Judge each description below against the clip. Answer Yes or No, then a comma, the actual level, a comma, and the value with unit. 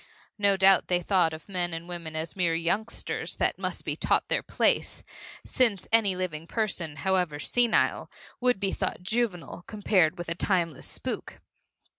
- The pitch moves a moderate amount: Yes, average, 3.3 semitones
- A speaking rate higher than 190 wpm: No, average, 160 wpm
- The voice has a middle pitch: Yes, medium, 180 Hz